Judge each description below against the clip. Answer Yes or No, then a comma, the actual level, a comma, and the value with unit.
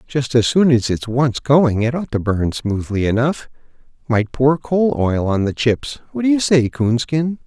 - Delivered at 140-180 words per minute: No, average, 195 wpm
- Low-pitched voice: Yes, low, 130 Hz